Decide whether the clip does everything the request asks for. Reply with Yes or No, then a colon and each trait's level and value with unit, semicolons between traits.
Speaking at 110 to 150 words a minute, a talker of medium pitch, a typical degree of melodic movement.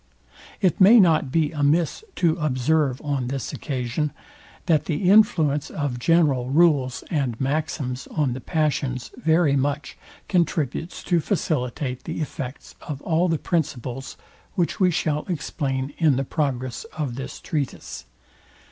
Yes: slow, 135 wpm; medium, 150 Hz; average, 3.6 semitones